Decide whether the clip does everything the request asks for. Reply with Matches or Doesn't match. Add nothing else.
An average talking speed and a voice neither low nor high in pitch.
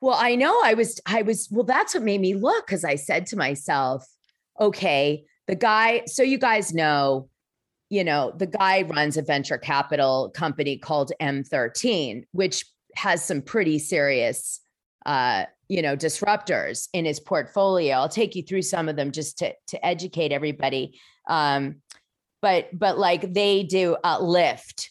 Matches